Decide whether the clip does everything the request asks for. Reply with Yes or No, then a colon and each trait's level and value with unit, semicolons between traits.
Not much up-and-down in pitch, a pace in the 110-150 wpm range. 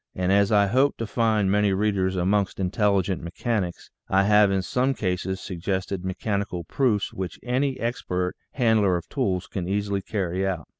No: narrow, 2.3 semitones; average, 160 wpm